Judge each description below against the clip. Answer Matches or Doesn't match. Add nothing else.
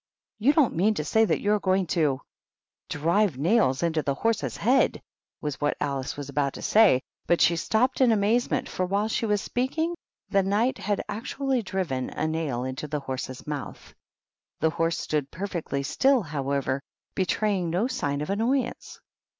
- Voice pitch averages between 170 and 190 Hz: Matches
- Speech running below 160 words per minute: Doesn't match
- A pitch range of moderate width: Doesn't match